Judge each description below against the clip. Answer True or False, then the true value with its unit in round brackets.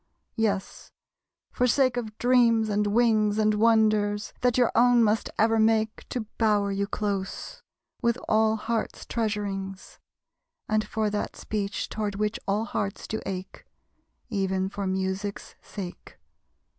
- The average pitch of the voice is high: True (215 Hz)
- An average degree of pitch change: False (1.9 semitones)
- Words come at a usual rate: False (130 wpm)